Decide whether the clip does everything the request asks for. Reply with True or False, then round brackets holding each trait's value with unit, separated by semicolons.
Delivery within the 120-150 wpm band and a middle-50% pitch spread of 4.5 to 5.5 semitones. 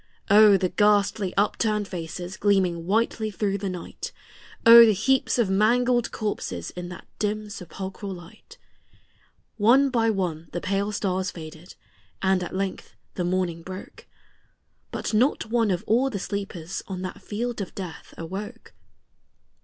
False (145 wpm; 2.9 semitones)